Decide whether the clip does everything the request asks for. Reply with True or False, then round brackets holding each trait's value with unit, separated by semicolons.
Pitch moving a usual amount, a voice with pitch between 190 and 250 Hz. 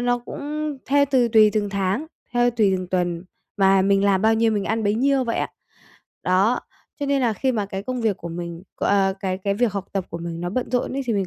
True (4.1 semitones; 210 Hz)